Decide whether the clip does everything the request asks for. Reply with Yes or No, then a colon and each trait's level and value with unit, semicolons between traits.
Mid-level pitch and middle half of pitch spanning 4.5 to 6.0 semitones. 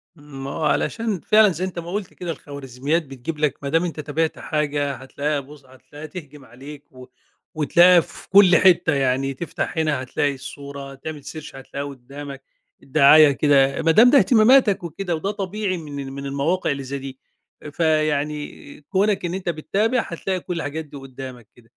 No: medium, 150 Hz; average, 3.9 semitones